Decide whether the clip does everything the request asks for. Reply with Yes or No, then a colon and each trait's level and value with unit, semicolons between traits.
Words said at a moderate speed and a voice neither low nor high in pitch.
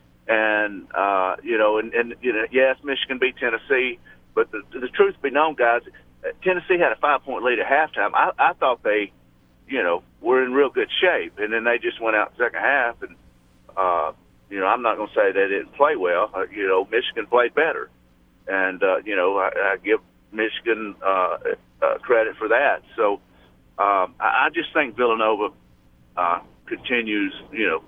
Yes: average, 185 wpm; medium, 145 Hz